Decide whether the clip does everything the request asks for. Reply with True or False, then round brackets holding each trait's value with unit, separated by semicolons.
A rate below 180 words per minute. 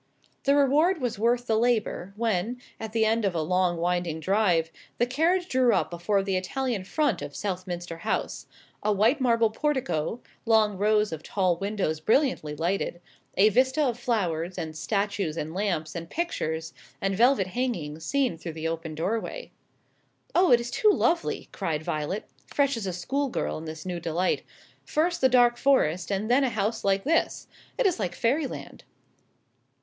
True (170 wpm)